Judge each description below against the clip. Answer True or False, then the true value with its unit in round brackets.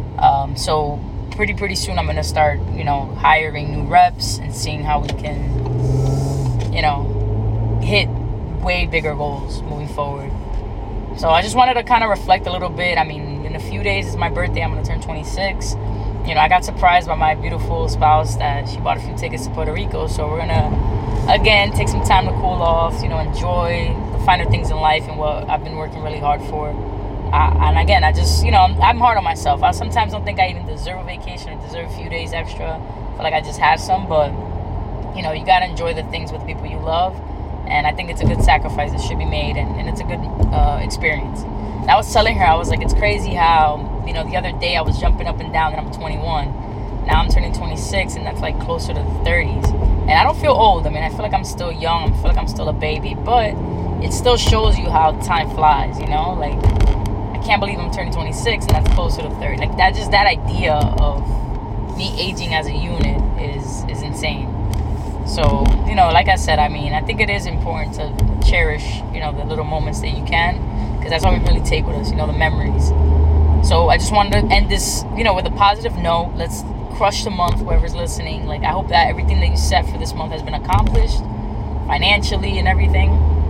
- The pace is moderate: False (230 wpm)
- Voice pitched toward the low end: True (100 Hz)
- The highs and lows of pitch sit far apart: True (6.7 semitones)